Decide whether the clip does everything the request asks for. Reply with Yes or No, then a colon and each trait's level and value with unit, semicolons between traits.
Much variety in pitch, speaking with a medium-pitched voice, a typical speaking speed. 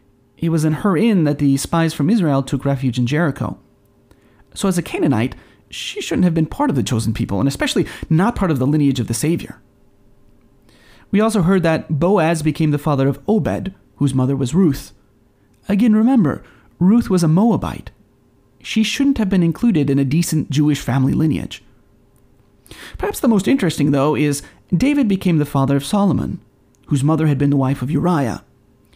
Yes: wide, 5.7 semitones; medium, 150 Hz; average, 180 wpm